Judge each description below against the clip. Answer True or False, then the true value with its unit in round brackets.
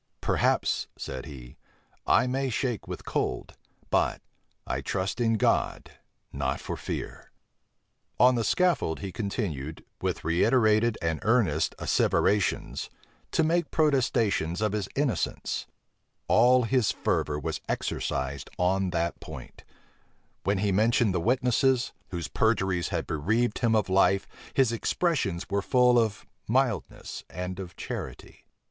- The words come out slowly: True (130 wpm)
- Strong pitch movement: True (5.9 semitones)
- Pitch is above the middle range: False (105 Hz)